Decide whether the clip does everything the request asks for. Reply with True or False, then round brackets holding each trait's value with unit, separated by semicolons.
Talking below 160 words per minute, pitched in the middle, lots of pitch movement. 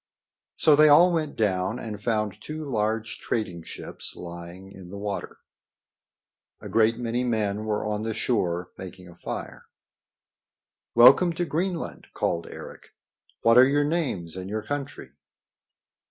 False (140 wpm; 110 Hz; 6.5 semitones)